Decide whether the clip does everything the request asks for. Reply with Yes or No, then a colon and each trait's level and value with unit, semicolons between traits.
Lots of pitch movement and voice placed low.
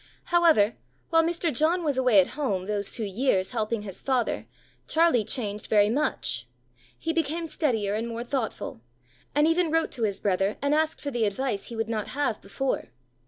No: wide, 6.7 semitones; high, 240 Hz